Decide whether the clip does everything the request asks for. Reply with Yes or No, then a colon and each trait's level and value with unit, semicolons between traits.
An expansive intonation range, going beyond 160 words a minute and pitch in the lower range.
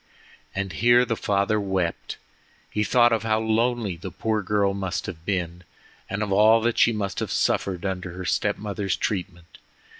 No: average, 2.8 semitones; average, 175 wpm; low, 100 Hz